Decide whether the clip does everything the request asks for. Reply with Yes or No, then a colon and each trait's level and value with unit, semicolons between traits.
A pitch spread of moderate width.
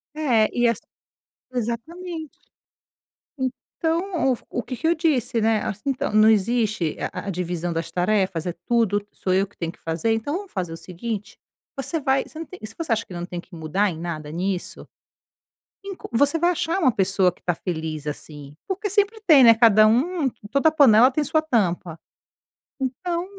No: wide, 8.9 semitones